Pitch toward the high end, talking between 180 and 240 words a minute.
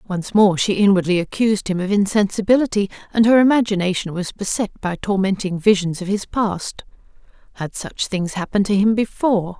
No: high, 200 Hz; average, 155 wpm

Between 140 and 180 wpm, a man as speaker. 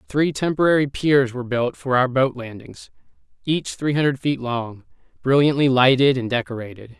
Yes: average, 155 wpm; male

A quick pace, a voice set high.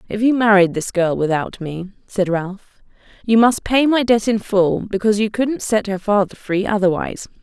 No: average, 195 wpm; high, 205 Hz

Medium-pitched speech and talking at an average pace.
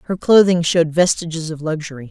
Yes: medium, 165 Hz; average, 170 wpm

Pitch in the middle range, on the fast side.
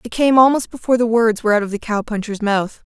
No: high, 225 Hz; fast, 250 wpm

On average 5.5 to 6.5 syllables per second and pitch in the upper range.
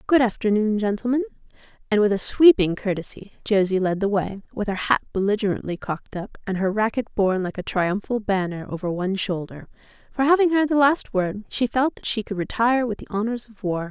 Yes: 5.8 syllables/s; high, 210 Hz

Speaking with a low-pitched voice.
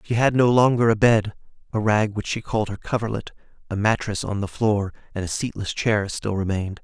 Yes: low, 105 Hz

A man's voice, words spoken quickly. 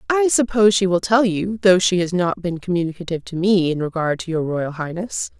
No: female; fast, 225 wpm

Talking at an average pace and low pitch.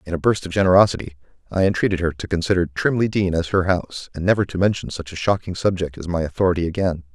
No: fast, 225 wpm; very low, 90 Hz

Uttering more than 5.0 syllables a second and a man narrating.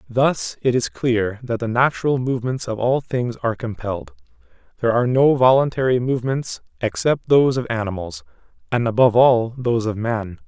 Yes: 5.6 syllables/s; male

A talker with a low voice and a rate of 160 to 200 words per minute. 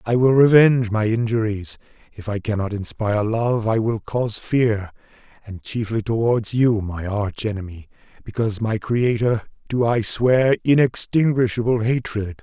No: low, 110 Hz; average, 140 wpm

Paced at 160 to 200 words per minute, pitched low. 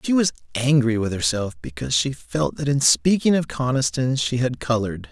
Yes: average, 190 wpm; low, 125 Hz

